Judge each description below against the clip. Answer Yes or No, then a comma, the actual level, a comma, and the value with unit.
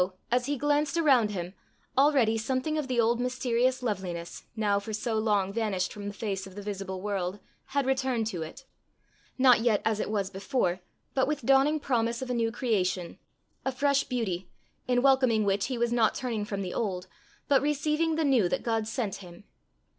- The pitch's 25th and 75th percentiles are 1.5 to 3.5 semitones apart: No, average, 4.7 semitones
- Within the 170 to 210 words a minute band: Yes, average, 190 wpm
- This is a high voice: Yes, high, 230 Hz